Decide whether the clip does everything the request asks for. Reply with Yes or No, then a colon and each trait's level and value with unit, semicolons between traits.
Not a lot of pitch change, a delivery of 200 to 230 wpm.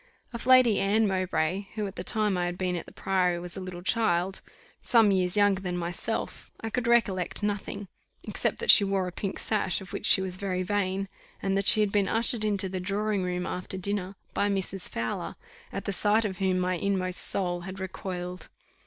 Yes: narrow, 2.1 semitones; fast, 205 wpm